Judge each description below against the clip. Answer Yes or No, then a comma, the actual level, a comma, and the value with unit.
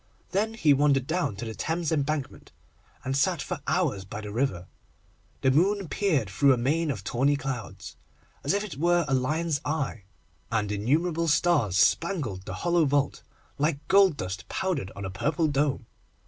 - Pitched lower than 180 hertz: Yes, medium, 140 Hz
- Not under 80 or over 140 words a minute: No, average, 170 wpm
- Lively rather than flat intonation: Yes, wide, 6.3 semitones